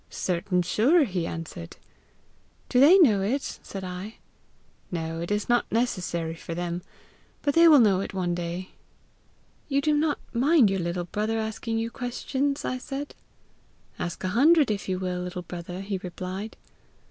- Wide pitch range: Yes, wide, 6.0 semitones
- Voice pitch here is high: Yes, high, 195 Hz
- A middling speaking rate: Yes, average, 160 wpm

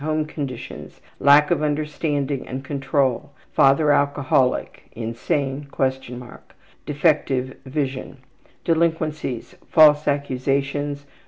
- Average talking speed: No, slow, 90 wpm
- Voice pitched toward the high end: No, medium, 145 Hz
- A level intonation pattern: Yes, narrow, 2.0 semitones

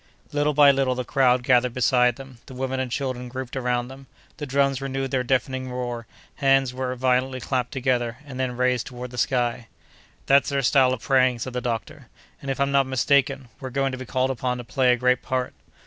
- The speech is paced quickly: Yes, fast, 210 wpm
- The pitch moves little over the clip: Yes, narrow, 1.4 semitones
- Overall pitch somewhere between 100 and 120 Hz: No, low, 130 Hz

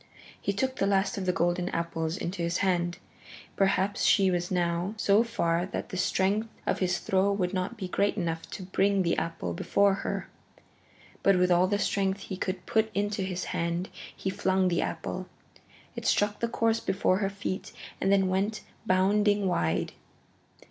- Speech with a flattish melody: Yes, narrow, 2.1 semitones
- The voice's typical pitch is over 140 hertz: Yes, high, 190 Hz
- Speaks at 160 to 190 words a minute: Yes, average, 175 wpm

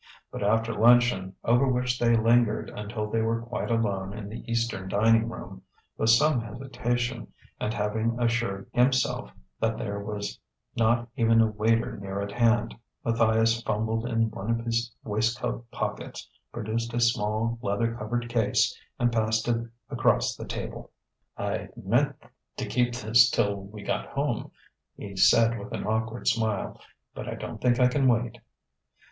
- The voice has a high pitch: No, low, 115 Hz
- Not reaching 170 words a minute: Yes, average, 155 wpm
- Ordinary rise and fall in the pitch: No, narrow, 1.8 semitones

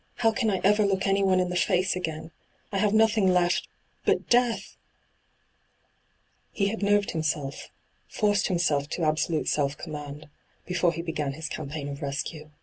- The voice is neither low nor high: Yes, medium, 175 Hz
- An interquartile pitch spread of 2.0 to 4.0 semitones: No, average, 4.6 semitones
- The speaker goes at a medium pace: Yes, average, 170 wpm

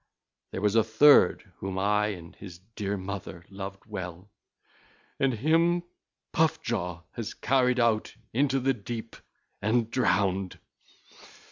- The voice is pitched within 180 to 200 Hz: No, low, 105 Hz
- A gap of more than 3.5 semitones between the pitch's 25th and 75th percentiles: Yes, average, 4.5 semitones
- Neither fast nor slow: No, slow, 125 wpm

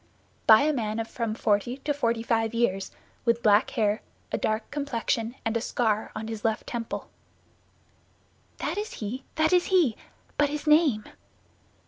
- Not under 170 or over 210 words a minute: No, average, 160 wpm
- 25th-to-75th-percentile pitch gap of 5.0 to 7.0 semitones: No, average, 4.5 semitones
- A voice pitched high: Yes, high, 230 Hz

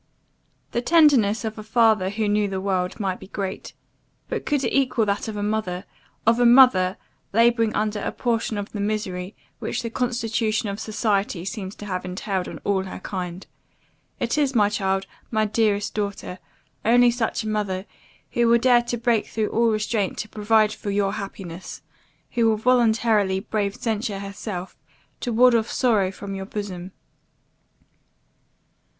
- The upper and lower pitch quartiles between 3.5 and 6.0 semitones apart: No, average, 2.8 semitones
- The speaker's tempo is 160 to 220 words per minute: Yes, average, 165 wpm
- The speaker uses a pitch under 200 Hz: No, high, 215 Hz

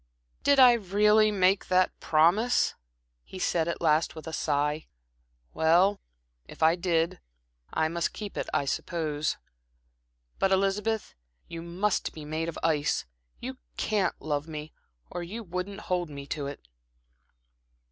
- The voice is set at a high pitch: No, medium, 170 Hz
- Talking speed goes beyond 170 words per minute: No, average, 140 wpm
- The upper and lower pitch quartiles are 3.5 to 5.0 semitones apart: Yes, average, 3.9 semitones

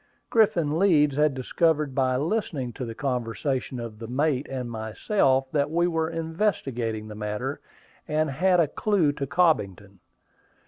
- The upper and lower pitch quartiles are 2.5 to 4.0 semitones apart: No, average, 5.1 semitones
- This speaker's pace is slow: No, average, 145 wpm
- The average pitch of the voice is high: No, medium, 140 Hz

